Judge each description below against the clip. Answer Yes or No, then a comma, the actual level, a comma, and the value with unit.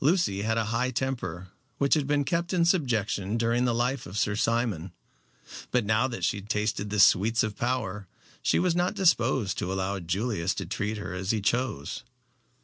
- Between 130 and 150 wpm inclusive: No, average, 185 wpm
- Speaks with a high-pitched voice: No, low, 115 Hz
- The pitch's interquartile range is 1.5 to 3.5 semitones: No, average, 4.6 semitones